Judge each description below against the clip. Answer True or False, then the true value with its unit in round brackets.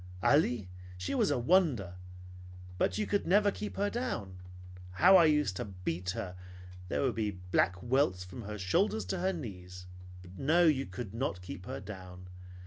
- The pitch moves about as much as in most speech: False (8.8 semitones)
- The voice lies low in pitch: True (105 Hz)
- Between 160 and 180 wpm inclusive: True (170 wpm)